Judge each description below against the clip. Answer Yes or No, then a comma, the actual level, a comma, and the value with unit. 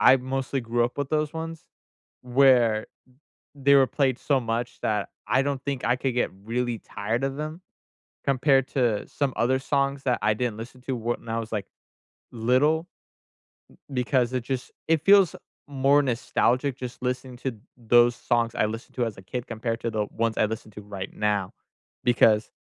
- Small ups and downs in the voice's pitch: No, average, 3.0 semitones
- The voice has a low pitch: Yes, low, 125 Hz